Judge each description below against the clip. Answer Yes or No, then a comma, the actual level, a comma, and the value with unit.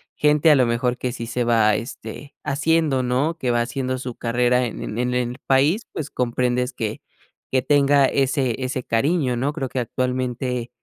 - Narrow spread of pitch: Yes, narrow, 2.3 semitones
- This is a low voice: Yes, low, 125 Hz